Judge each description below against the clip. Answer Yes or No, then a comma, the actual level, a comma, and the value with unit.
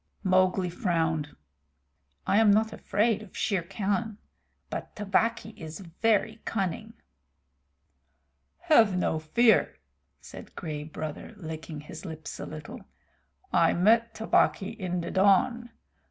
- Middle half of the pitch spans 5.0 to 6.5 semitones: Yes, average, 5.3 semitones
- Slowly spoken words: Yes, slow, 115 wpm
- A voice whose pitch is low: No, high, 190 Hz